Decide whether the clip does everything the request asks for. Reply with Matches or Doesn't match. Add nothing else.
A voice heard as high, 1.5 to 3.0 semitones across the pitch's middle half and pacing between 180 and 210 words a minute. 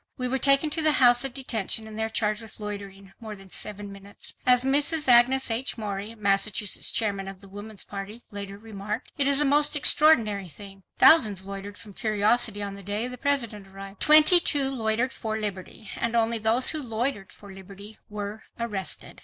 Doesn't match